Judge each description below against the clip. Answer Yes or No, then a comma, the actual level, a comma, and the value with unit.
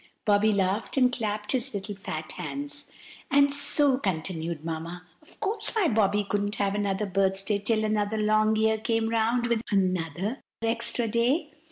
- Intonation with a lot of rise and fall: No, average, 3.3 semitones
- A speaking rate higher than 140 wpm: Yes, average, 155 wpm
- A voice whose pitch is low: No, high, 215 Hz